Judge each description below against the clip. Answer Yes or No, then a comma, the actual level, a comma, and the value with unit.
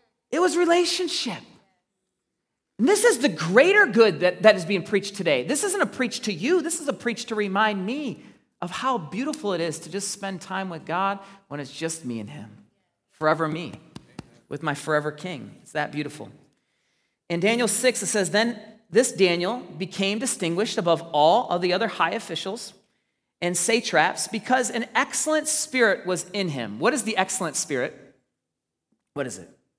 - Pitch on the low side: No, high, 200 Hz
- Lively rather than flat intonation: Yes, wide, 6.0 semitones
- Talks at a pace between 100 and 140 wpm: No, average, 175 wpm